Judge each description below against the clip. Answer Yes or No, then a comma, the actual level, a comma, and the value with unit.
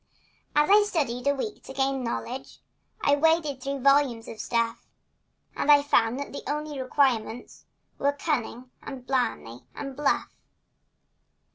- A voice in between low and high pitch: No, very high, 275 Hz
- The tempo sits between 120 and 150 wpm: Yes, average, 140 wpm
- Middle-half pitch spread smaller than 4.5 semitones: Yes, average, 2.8 semitones